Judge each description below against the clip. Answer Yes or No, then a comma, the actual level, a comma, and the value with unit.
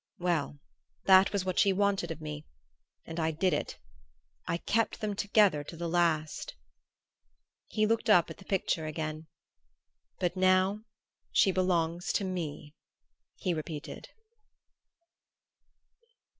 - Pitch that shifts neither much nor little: Yes, average, 3.4 semitones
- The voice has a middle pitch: Yes, medium, 175 Hz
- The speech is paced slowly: Yes, slow, 125 wpm